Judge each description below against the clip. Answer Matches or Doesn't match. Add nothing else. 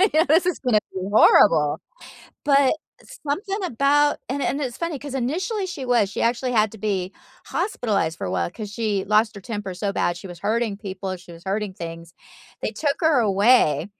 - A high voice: Matches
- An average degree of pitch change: Doesn't match